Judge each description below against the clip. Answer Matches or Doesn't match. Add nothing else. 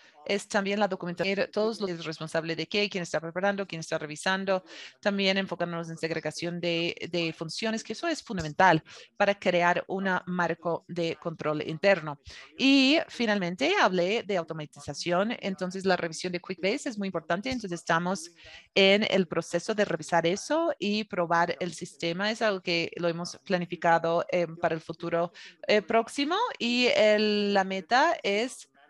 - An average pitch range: Matches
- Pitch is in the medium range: Matches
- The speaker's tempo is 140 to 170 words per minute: Matches